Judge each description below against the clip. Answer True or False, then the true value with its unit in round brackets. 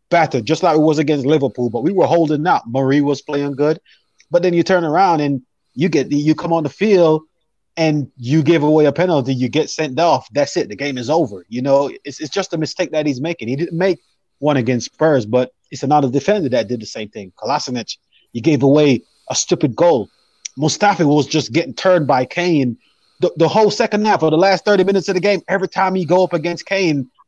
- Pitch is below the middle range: False (155 Hz)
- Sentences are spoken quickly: True (230 wpm)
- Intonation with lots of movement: False (3.6 semitones)